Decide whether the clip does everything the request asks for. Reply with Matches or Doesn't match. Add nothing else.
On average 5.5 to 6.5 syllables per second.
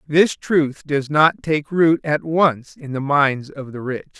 Doesn't match